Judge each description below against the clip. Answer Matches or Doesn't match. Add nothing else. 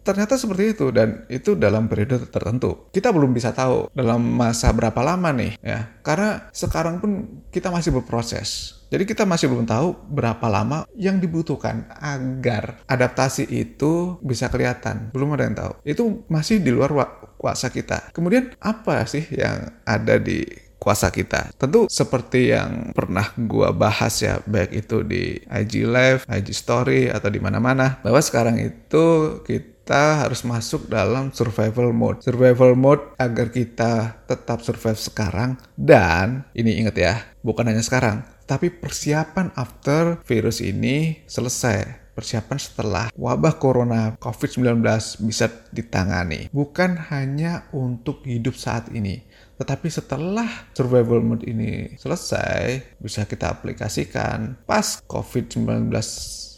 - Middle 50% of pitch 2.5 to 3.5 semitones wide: Doesn't match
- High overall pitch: Doesn't match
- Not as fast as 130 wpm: Doesn't match